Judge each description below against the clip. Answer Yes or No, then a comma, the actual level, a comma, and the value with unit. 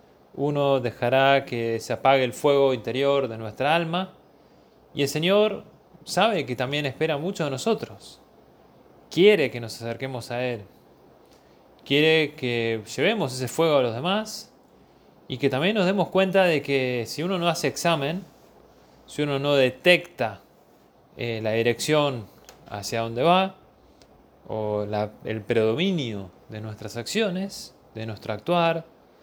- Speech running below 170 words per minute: Yes, average, 140 wpm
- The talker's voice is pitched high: No, medium, 140 Hz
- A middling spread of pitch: No, wide, 6.6 semitones